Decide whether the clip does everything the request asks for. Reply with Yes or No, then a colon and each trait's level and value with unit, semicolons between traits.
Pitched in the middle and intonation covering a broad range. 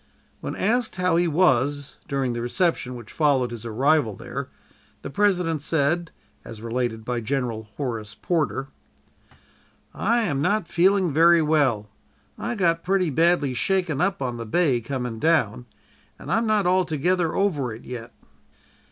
Yes: medium, 150 Hz; wide, 6.4 semitones